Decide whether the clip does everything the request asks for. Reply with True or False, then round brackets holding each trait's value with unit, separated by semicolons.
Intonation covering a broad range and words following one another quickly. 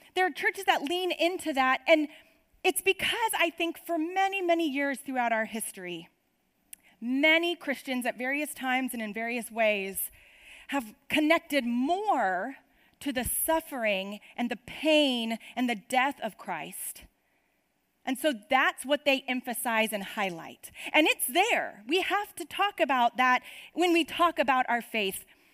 False (5.7 semitones; 155 wpm)